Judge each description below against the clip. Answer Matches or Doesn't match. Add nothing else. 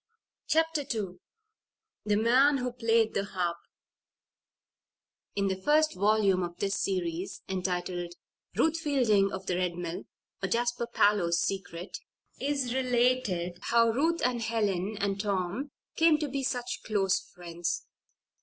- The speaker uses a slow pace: Matches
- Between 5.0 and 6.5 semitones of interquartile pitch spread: Matches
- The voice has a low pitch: Doesn't match